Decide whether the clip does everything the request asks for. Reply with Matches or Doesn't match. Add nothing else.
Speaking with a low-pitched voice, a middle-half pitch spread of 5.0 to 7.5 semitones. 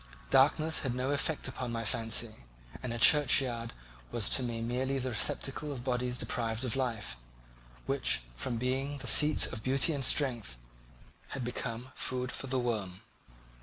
Doesn't match